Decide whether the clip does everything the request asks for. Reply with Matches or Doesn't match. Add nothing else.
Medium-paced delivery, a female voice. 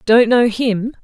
Matches